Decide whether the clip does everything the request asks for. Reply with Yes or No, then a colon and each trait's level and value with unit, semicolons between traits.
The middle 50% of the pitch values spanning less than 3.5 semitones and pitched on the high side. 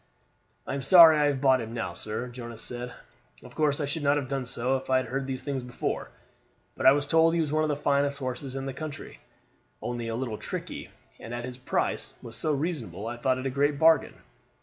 No: average, 2.9 semitones; low, 135 Hz